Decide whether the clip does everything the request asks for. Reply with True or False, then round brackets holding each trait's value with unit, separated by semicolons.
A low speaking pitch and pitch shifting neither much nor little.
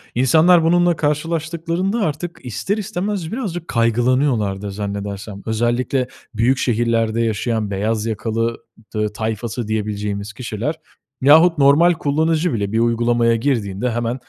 False (120 Hz; 6.5 semitones)